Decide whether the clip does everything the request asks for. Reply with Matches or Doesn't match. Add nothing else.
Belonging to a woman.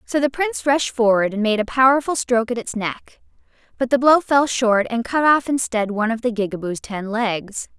Matches